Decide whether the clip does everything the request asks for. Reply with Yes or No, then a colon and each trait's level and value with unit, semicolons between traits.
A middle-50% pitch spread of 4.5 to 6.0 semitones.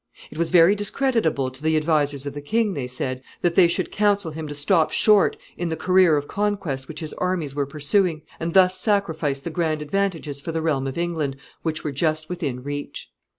No: average, 4.1 semitones